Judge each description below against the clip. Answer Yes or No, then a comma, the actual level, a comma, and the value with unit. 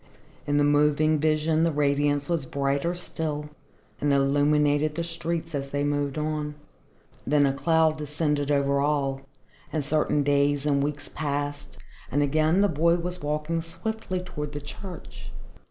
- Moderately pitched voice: Yes, medium, 150 Hz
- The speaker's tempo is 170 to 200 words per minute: No, average, 150 wpm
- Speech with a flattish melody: Yes, narrow, 1.8 semitones